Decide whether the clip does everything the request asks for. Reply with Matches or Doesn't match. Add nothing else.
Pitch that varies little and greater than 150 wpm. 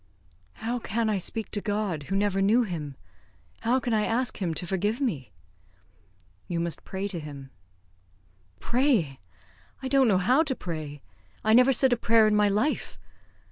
Doesn't match